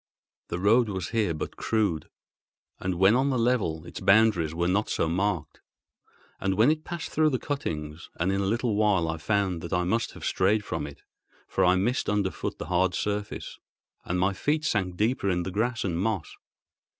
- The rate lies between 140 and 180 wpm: No, average, 195 wpm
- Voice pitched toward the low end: Yes, low, 100 Hz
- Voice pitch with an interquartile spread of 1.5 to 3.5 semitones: No, average, 4.1 semitones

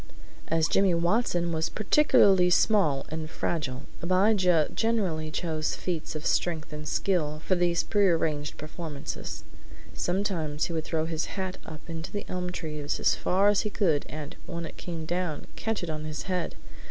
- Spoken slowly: No, average, 165 wpm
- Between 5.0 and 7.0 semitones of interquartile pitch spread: No, average, 3.0 semitones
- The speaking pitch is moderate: Yes, medium, 170 Hz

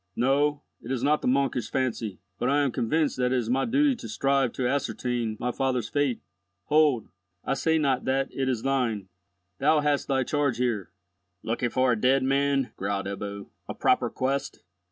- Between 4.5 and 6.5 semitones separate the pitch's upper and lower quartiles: No, average, 2.7 semitones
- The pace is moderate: Yes, average, 185 wpm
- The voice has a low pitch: Yes, low, 130 Hz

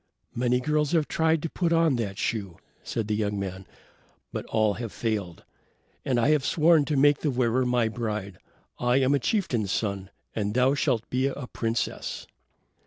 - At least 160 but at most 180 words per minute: Yes, average, 175 wpm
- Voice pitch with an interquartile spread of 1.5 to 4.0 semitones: No, average, 5.1 semitones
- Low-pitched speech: Yes, low, 125 Hz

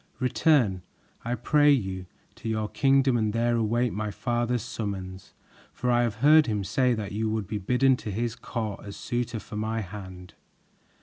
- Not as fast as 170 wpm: No, average, 175 wpm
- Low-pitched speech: Yes, low, 115 Hz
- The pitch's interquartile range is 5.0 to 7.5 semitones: No, average, 3.0 semitones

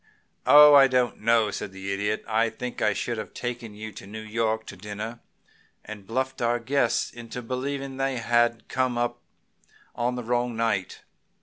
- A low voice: Yes, low, 115 Hz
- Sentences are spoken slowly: No, average, 175 wpm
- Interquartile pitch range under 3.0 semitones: Yes, narrow, 2.4 semitones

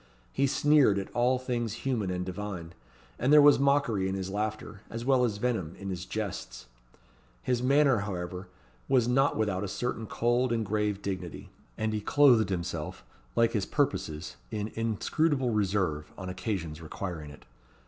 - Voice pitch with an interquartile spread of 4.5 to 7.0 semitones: Yes, average, 4.8 semitones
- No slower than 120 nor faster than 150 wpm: No, average, 160 wpm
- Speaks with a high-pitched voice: No, low, 105 Hz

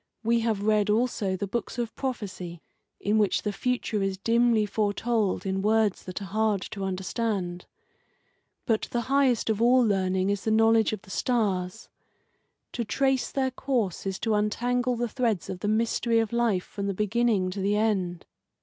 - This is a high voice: Yes, high, 215 Hz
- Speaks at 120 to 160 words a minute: No, average, 175 wpm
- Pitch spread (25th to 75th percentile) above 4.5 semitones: No, average, 3.2 semitones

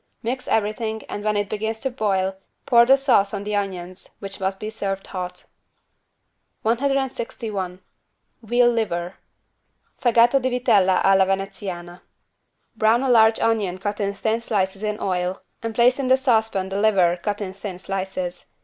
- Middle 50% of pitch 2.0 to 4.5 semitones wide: Yes, average, 3.3 semitones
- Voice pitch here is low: No, high, 205 Hz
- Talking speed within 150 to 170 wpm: Yes, average, 155 wpm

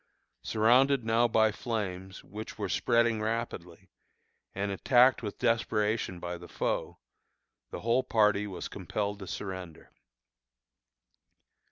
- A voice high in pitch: No, low, 105 Hz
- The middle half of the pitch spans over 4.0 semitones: No, average, 3.5 semitones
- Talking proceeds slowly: Yes, slow, 120 wpm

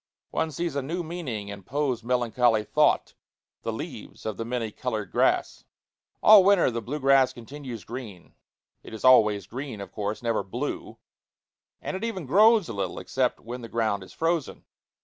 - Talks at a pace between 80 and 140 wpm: No, average, 170 wpm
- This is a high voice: No, low, 125 Hz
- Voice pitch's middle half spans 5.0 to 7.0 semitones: Yes, average, 5.3 semitones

